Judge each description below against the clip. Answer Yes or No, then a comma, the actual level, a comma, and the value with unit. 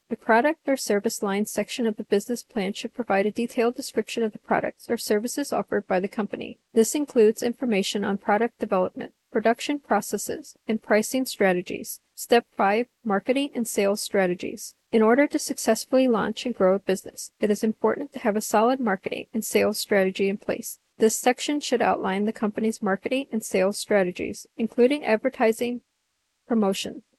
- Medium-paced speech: Yes, average, 170 wpm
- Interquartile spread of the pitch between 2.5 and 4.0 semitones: Yes, average, 2.8 semitones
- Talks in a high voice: Yes, high, 225 Hz